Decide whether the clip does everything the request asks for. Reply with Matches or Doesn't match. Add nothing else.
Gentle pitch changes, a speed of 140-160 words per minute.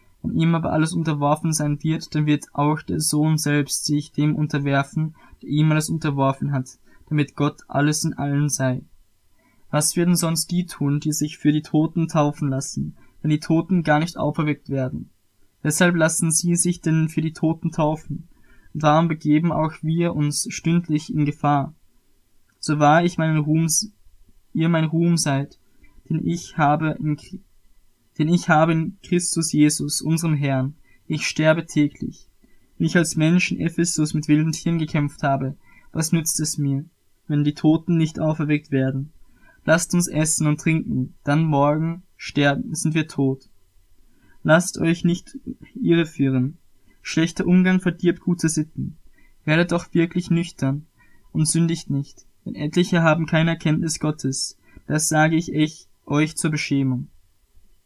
Matches